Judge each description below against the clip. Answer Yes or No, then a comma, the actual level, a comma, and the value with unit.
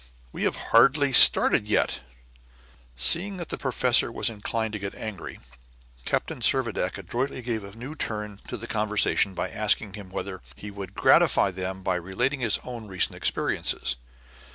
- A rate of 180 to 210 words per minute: No, average, 155 wpm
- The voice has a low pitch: Yes, low, 110 Hz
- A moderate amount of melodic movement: Yes, average, 3.8 semitones